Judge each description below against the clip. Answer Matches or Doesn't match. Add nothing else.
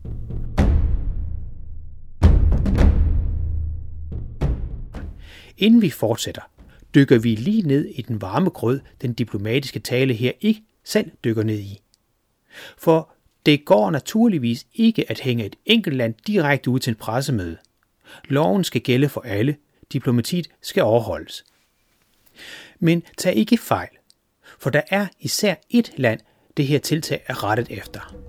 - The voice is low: Matches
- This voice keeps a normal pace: Doesn't match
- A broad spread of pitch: Matches